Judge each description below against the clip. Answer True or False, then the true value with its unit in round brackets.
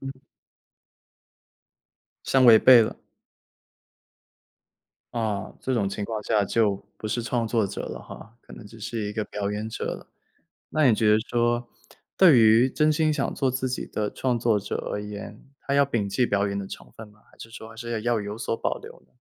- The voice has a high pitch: False (115 Hz)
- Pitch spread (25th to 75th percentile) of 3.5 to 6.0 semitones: False (2.7 semitones)